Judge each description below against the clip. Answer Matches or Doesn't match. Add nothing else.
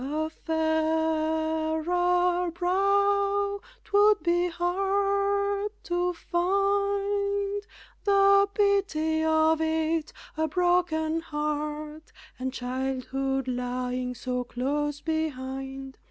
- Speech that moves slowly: Matches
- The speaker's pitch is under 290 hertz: Doesn't match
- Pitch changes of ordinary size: Matches